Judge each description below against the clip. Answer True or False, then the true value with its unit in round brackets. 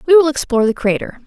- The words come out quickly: True (235 wpm)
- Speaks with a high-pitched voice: True (265 Hz)